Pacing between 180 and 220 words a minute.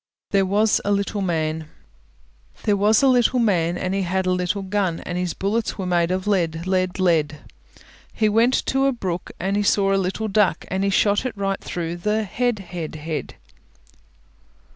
Yes: average, 185 wpm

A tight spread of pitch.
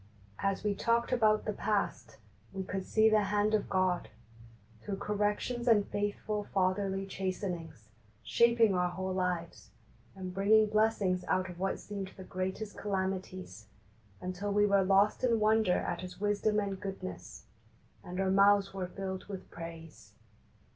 Yes: narrow, 2.0 semitones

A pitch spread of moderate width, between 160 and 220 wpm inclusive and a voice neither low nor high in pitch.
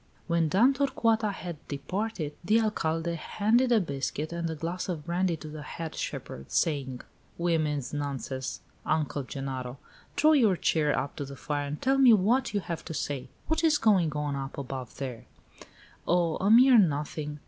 No: wide, 6.5 semitones; average, 170 wpm; medium, 165 Hz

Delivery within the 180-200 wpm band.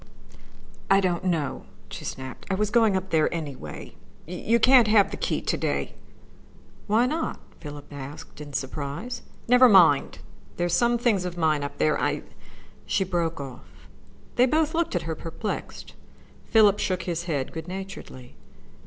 No: average, 160 wpm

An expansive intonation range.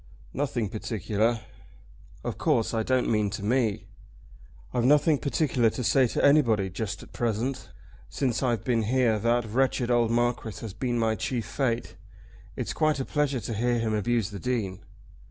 No: average, 2.7 semitones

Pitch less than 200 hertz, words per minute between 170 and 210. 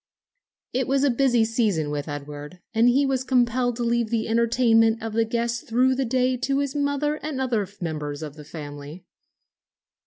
No: high, 235 Hz; average, 180 wpm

